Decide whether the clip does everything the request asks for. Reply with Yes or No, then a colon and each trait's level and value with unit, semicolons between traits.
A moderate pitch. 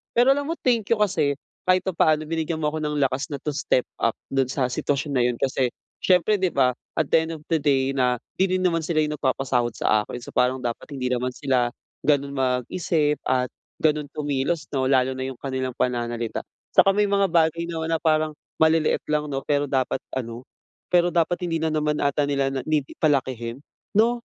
Yes: medium, 145 Hz